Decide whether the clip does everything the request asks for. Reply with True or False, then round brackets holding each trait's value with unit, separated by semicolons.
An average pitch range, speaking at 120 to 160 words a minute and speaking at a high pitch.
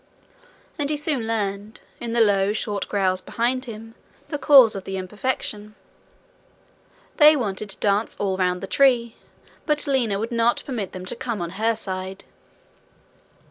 True (3.8 semitones; 155 wpm; 215 Hz)